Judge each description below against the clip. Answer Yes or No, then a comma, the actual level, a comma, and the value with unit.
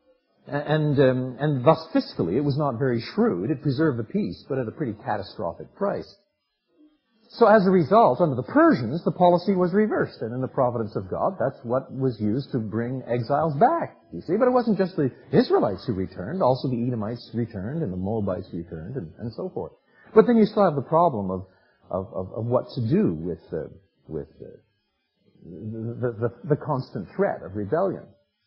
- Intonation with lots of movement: Yes, wide, 7.8 semitones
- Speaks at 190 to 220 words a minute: Yes, average, 195 wpm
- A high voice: No, low, 135 Hz